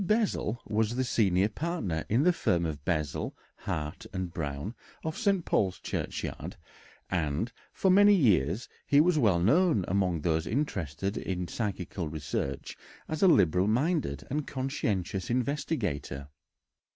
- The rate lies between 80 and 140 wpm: Yes, slow, 135 wpm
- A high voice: No, low, 100 Hz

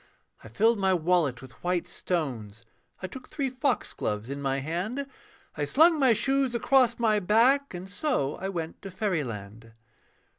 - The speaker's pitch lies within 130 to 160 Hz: No, medium, 185 Hz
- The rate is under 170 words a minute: Yes, average, 155 wpm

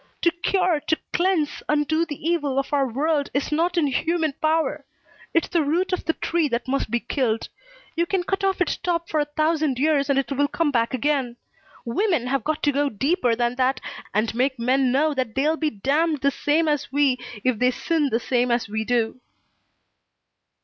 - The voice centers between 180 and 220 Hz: No, very high, 290 Hz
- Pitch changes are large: No, average, 4.1 semitones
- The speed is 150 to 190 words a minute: No, average, 200 wpm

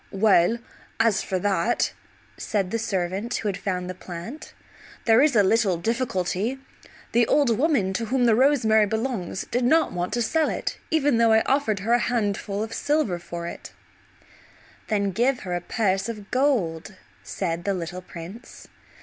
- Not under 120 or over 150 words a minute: No, average, 165 wpm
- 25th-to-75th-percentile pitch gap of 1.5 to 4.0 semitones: No, average, 4.4 semitones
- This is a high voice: Yes, high, 215 Hz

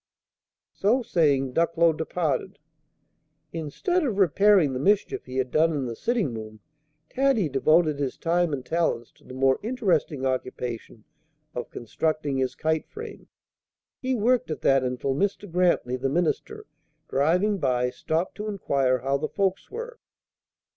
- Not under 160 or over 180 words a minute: No, average, 145 wpm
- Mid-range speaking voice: Yes, medium, 160 Hz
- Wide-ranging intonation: Yes, wide, 6.9 semitones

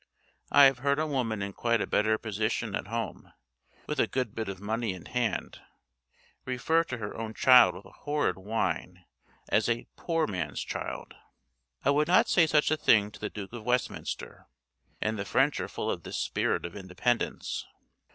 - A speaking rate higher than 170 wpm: Yes, average, 185 wpm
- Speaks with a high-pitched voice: No, low, 115 Hz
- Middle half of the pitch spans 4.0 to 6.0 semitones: Yes, average, 4.6 semitones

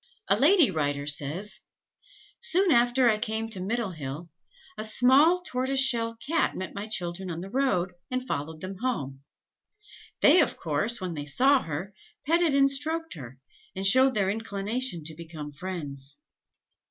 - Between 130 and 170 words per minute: Yes, average, 155 wpm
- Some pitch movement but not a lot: No, wide, 7.9 semitones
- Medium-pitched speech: No, high, 205 Hz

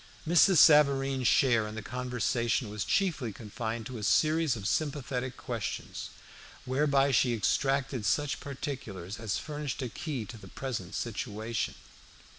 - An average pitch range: Yes, average, 4.1 semitones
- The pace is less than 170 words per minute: Yes, slow, 135 wpm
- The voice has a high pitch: No, low, 125 Hz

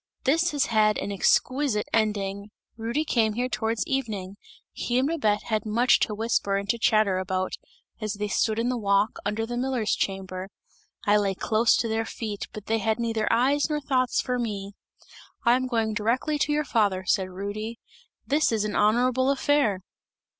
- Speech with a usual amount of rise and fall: Yes, average, 3.4 semitones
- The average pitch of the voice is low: No, high, 220 Hz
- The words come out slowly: No, average, 180 wpm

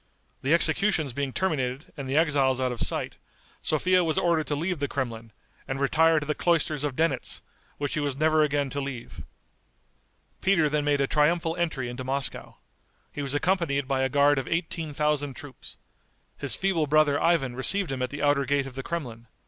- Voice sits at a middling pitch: Yes, medium, 145 Hz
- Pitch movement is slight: No, average, 3.0 semitones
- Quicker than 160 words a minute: Yes, average, 190 wpm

